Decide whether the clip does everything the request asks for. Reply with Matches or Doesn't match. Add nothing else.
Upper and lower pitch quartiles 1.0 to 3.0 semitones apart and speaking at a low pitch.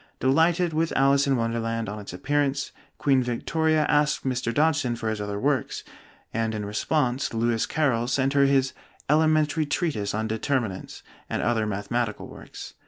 Doesn't match